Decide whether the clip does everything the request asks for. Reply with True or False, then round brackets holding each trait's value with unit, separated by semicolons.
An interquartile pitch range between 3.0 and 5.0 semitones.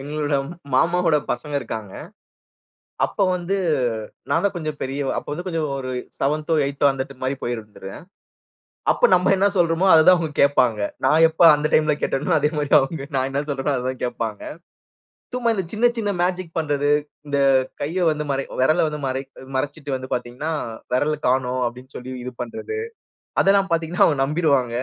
True (3.9 semitones)